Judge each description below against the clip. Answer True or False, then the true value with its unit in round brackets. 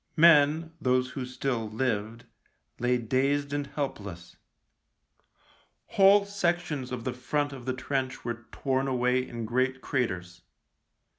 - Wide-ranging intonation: False (3.1 semitones)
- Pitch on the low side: True (130 Hz)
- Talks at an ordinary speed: False (130 wpm)